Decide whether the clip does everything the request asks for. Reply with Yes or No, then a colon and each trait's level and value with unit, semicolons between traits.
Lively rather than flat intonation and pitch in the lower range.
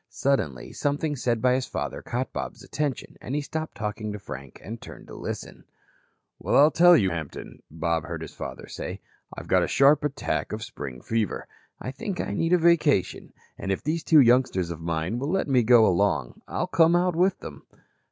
Yes: wide, 8.4 semitones; low, 125 Hz